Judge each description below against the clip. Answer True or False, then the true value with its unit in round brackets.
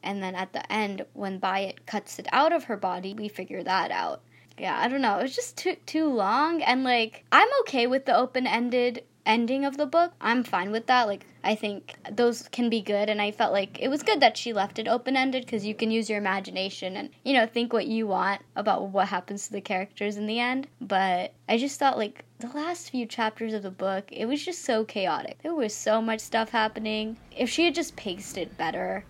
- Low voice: False (225 Hz)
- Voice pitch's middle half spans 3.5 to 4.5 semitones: True (4.2 semitones)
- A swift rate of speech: True (235 wpm)